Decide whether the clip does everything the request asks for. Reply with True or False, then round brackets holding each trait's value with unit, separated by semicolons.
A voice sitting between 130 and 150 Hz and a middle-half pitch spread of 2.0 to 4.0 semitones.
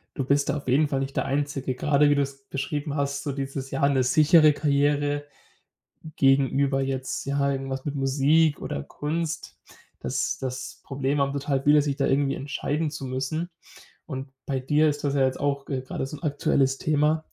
False (140 Hz; 1.5 semitones)